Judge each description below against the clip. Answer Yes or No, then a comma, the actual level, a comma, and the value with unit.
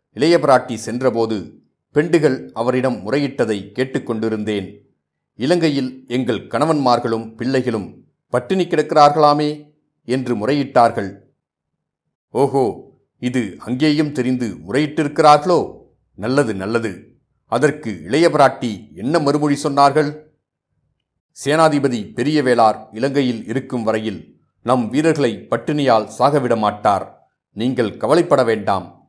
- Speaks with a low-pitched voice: Yes, low, 130 Hz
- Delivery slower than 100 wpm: Yes, average, 80 wpm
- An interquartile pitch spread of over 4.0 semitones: Yes, average, 4.5 semitones